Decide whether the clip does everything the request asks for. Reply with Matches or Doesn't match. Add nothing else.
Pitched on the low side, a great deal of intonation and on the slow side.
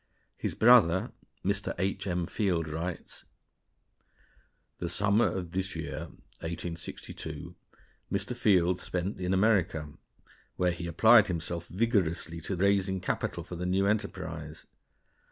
Doesn't match